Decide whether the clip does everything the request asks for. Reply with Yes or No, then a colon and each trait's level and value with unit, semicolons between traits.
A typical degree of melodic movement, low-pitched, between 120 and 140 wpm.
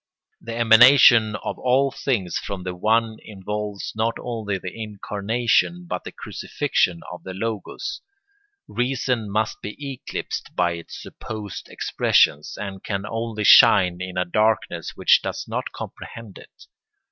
Yes: average, 3.2 semitones; low, 110 Hz; slow, 135 wpm